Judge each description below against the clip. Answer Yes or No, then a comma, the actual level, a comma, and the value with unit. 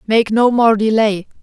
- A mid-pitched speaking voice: No, high, 220 Hz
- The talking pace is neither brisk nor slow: Yes, average, 170 wpm